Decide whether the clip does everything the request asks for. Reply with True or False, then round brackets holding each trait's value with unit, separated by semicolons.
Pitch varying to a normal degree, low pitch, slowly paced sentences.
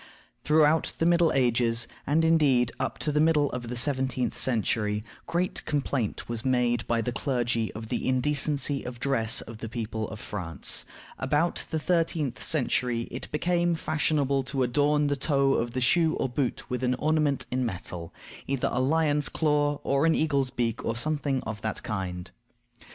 False (4.0 semitones; 130 Hz; 175 wpm)